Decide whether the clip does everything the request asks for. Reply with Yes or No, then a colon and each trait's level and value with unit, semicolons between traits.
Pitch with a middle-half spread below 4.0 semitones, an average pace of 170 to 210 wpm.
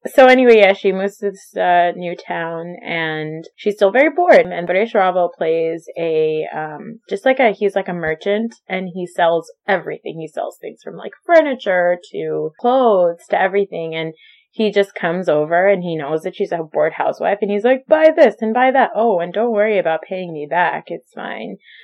No: average, 5.0 semitones; average, 200 wpm